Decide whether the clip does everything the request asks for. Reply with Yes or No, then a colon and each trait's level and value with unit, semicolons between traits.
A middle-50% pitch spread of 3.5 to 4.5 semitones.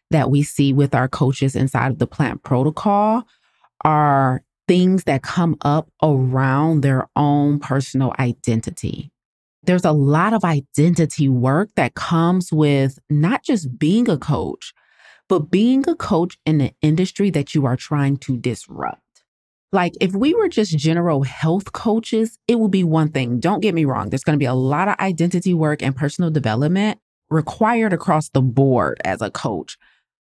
No: average, 5.2 semitones